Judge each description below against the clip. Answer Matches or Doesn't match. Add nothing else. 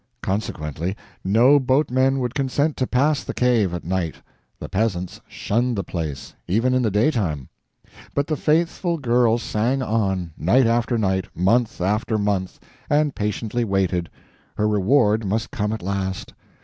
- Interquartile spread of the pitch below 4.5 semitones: Doesn't match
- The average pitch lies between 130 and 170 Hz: Doesn't match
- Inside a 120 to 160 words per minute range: Matches